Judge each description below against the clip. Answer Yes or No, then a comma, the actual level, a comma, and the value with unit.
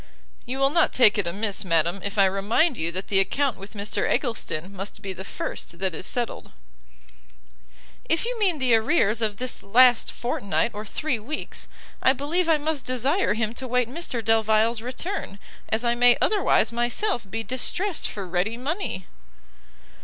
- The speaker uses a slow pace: No, average, 170 wpm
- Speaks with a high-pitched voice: Yes, high, 230 Hz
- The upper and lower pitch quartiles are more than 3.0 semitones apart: Yes, average, 5.2 semitones